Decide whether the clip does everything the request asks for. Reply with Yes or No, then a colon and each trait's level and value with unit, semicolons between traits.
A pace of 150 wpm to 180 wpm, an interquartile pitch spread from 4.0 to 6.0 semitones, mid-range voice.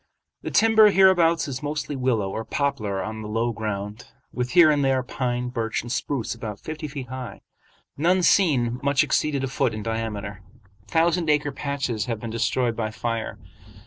No: average, 175 wpm; average, 4.8 semitones; low, 125 Hz